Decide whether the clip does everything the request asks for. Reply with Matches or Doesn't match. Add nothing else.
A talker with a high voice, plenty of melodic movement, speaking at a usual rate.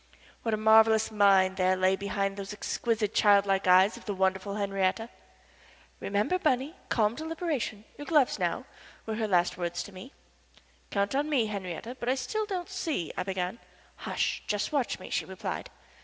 Doesn't match